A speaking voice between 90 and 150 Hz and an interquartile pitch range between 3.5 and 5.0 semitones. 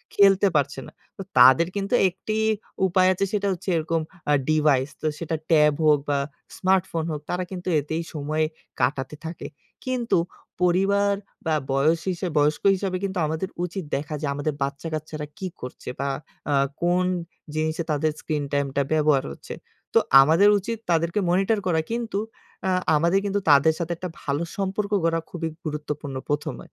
No: medium, 165 Hz; average, 4.1 semitones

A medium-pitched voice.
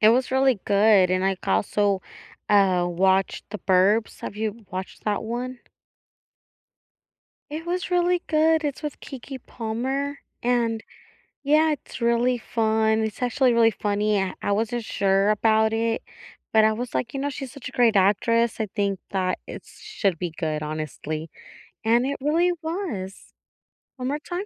No: high, 225 Hz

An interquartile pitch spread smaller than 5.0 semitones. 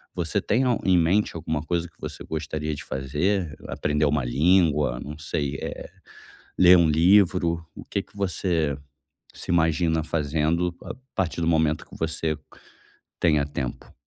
Yes: average, 2.7 semitones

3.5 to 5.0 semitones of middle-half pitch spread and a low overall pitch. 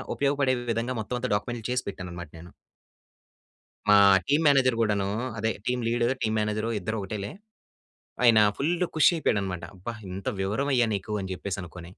Yes: average, 4.5 semitones; low, 110 Hz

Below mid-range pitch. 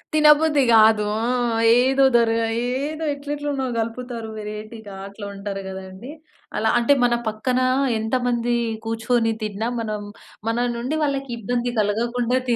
No: high, 235 Hz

